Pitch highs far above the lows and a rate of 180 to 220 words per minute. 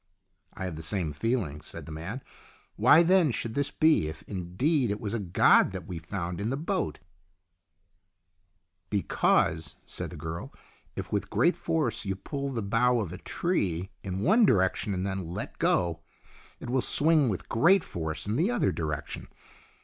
Yes: wide, 7.3 semitones; average, 190 wpm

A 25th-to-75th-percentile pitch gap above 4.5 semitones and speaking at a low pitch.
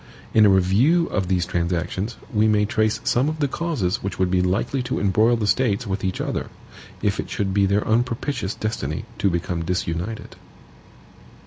No: average, 4.1 semitones; low, 105 Hz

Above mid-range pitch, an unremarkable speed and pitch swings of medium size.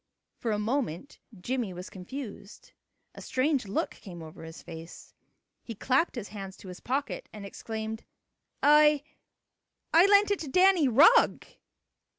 No: high, 235 Hz; average, 145 wpm; wide, 7.1 semitones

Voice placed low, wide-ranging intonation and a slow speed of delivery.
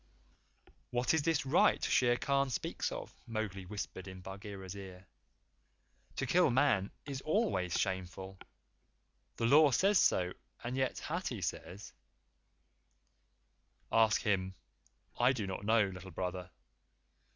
Yes: low, 105 Hz; wide, 5.8 semitones; slow, 125 wpm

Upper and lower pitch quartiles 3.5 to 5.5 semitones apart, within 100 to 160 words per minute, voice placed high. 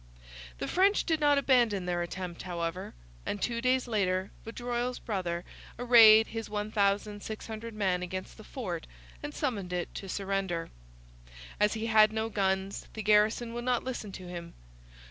Yes: average, 3.9 semitones; average, 150 wpm; high, 210 Hz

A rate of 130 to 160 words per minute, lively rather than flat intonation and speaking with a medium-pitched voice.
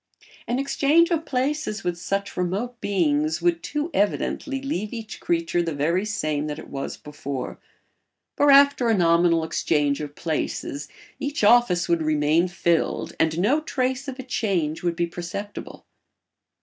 Yes: average, 150 wpm; wide, 7.6 semitones; medium, 180 Hz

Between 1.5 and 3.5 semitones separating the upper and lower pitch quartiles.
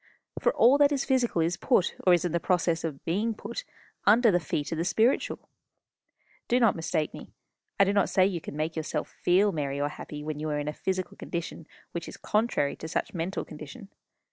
No: average, 4.8 semitones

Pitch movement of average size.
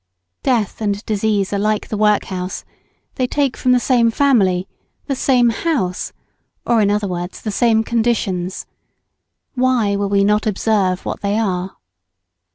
Yes: average, 3.2 semitones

